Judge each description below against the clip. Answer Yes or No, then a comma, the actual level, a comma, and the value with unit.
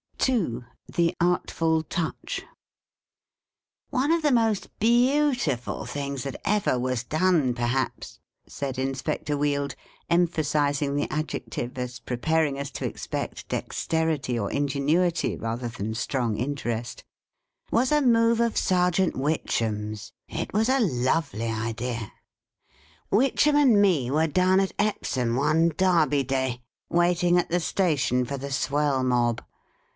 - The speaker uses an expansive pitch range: Yes, wide, 6.3 semitones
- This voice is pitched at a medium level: Yes, medium, 145 Hz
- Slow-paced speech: Yes, slow, 130 wpm